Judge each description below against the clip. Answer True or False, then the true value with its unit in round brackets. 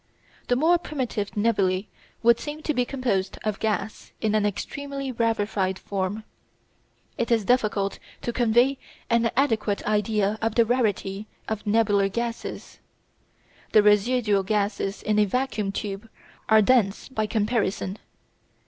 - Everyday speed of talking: False (130 wpm)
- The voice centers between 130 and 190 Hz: False (215 Hz)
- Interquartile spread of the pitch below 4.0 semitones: True (2.8 semitones)